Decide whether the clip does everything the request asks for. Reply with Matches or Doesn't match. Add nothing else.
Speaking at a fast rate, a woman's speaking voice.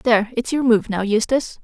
Matches